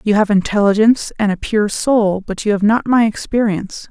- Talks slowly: No, average, 200 wpm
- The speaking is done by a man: No, female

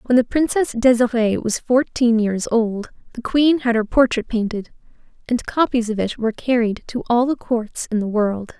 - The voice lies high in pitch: Yes, high, 235 Hz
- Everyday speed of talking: Yes, average, 190 wpm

